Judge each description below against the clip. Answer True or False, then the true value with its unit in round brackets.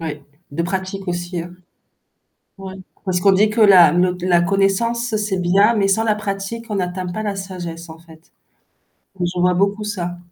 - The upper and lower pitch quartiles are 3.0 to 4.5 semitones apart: False (2.6 semitones)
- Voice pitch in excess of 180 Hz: True (190 Hz)